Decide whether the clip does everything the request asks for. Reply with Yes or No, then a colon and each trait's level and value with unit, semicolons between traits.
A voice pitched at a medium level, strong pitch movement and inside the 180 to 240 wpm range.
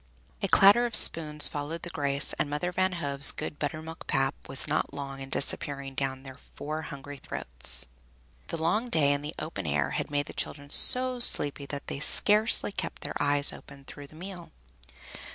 No: medium, 145 Hz; average, 3.2 semitones; average, 185 wpm